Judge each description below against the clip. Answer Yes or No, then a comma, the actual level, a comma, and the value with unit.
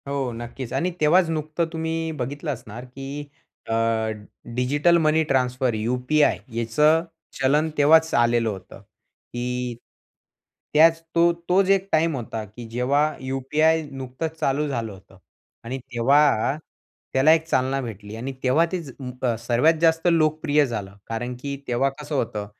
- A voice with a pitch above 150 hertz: No, low, 135 Hz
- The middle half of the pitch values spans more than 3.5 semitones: Yes, average, 4.5 semitones